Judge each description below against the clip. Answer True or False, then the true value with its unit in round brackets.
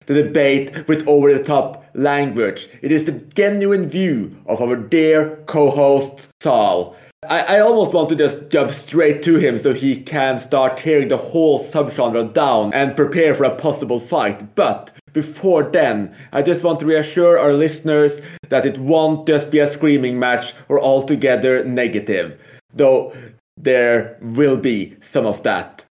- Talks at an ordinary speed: True (160 wpm)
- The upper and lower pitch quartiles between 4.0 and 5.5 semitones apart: False (3.0 semitones)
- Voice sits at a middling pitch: True (145 Hz)